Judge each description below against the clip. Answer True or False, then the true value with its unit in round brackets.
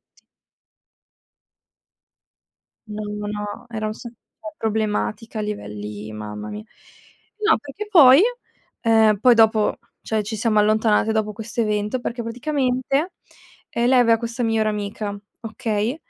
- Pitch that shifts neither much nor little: False (2.3 semitones)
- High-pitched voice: True (220 Hz)